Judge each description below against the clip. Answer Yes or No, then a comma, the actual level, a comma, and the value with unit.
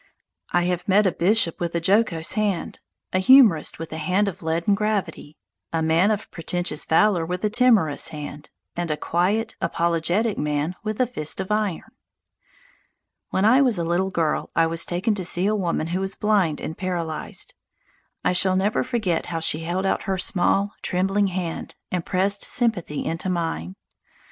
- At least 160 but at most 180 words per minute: Yes, average, 175 wpm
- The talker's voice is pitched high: No, medium, 180 Hz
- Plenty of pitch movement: No, average, 3.7 semitones